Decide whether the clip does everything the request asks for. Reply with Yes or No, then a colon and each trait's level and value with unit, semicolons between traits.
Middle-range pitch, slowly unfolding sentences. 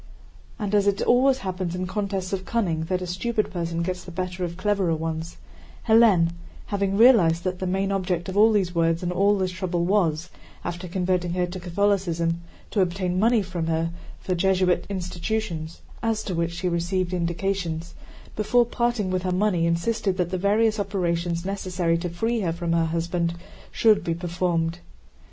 No: medium, 180 Hz; average, 170 wpm